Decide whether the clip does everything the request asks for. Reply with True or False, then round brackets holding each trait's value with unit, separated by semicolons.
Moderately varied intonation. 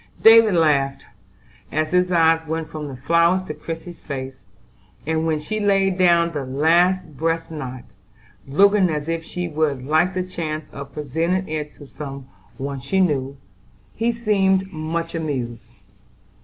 True (3.8 semitones)